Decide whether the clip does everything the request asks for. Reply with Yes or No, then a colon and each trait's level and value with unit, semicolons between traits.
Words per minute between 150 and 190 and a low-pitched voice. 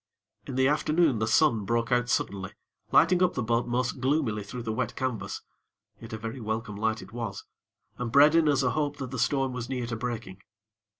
No: fast, 205 wpm; low, 125 Hz